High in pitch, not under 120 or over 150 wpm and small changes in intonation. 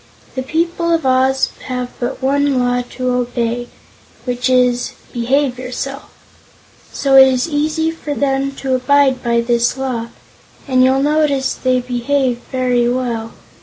Yes: very high, 255 Hz; average, 140 wpm; narrow, 2.0 semitones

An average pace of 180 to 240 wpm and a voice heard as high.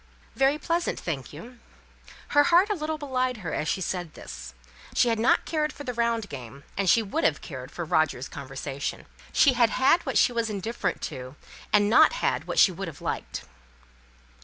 Yes: average, 190 wpm; high, 220 Hz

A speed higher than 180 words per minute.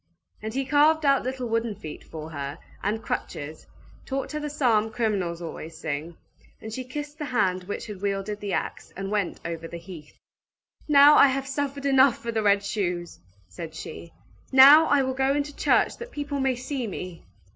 Yes: average, 190 wpm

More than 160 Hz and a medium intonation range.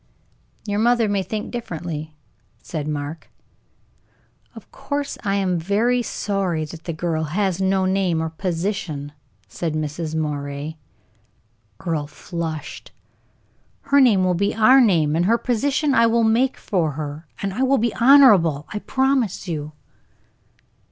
No: medium, 185 Hz; wide, 6.1 semitones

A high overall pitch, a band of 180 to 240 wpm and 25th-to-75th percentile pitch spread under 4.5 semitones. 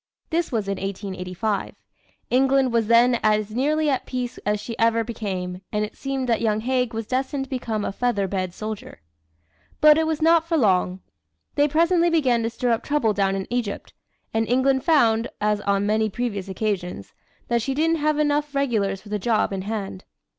No: high, 230 Hz; average, 190 wpm; average, 4.8 semitones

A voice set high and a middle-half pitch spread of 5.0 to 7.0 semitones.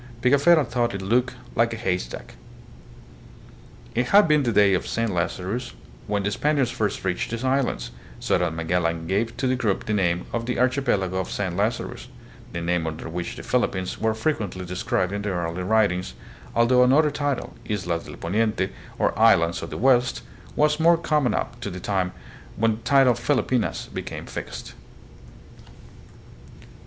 No: low, 110 Hz; wide, 5.6 semitones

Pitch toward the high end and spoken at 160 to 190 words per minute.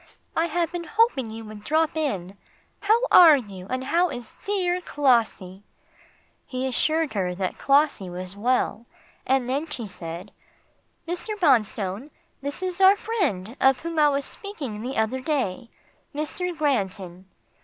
No: very high, 265 Hz; average, 145 wpm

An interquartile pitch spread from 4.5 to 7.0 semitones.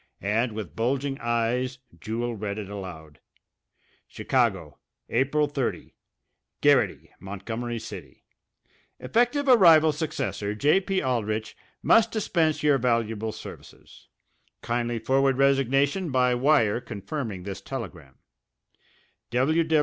Yes: average, 4.8 semitones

